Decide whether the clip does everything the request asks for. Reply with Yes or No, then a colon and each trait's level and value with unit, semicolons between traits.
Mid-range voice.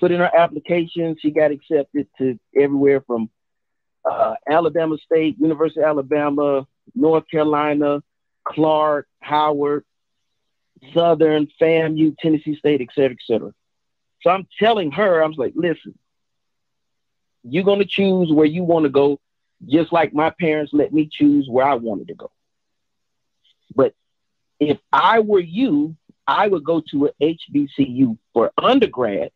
Yes: medium, 155 Hz